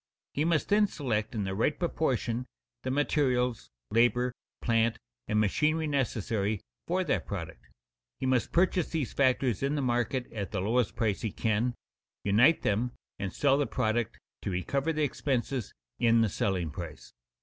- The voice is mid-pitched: No, low, 120 Hz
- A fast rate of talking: No, average, 160 wpm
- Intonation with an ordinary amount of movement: Yes, average, 4.7 semitones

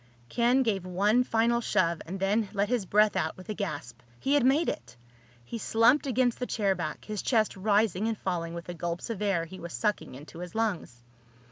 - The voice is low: No, high, 205 Hz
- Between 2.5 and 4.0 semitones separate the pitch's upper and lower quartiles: No, average, 4.5 semitones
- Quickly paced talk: Yes, fast, 210 wpm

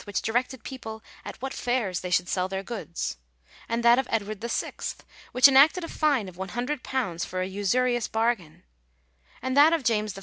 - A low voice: No, high, 230 Hz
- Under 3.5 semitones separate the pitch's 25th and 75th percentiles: No, average, 5.0 semitones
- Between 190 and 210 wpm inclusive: No, average, 180 wpm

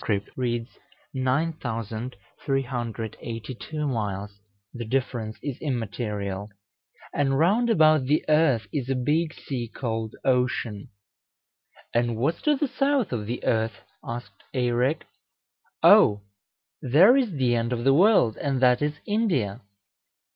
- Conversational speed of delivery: No, slow, 120 wpm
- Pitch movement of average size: Yes, average, 4.8 semitones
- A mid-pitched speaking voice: No, low, 125 Hz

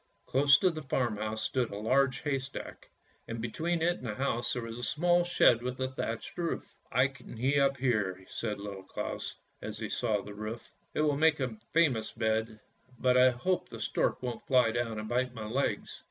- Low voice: Yes, low, 125 Hz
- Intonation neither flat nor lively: Yes, average, 3.8 semitones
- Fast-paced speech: Yes, fast, 210 wpm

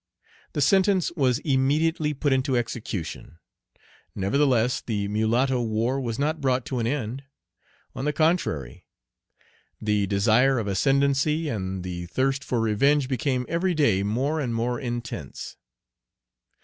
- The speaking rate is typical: No, slow, 130 wpm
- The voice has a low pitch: Yes, low, 130 Hz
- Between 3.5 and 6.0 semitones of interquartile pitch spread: Yes, average, 4.5 semitones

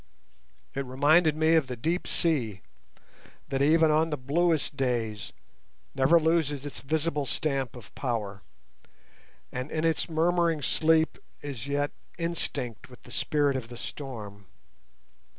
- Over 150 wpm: No, slow, 135 wpm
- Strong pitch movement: No, average, 4.1 semitones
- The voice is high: No, medium, 145 Hz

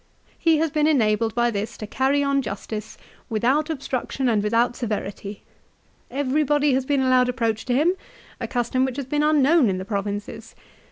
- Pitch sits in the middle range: No, very high, 255 Hz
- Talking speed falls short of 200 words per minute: Yes, average, 180 wpm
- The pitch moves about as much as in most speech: Yes, average, 4.6 semitones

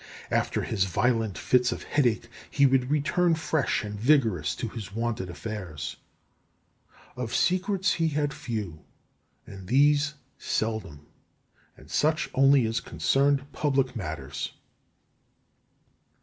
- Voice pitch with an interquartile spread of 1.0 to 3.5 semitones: No, wide, 5.5 semitones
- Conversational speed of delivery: No, slow, 115 wpm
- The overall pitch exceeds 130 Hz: No, low, 125 Hz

